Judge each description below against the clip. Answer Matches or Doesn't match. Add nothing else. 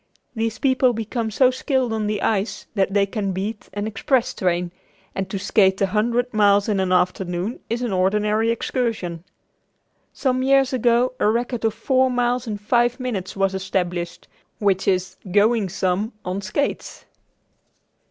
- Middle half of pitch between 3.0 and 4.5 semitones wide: Matches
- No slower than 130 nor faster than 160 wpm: Matches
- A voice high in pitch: Matches